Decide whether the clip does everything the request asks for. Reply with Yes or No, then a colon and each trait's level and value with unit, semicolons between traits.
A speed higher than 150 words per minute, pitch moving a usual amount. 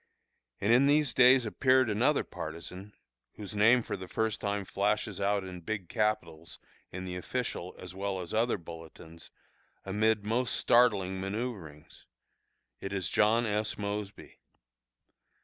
No: slow, 135 wpm; average, 3.3 semitones